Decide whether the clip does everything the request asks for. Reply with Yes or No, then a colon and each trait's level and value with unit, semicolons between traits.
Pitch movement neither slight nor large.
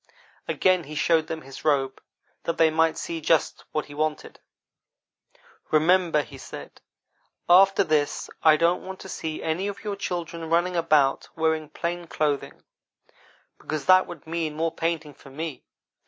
No: narrow, 2.1 semitones